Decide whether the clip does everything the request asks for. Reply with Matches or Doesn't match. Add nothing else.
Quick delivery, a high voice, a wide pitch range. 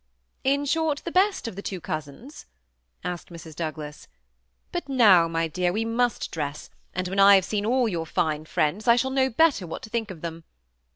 Matches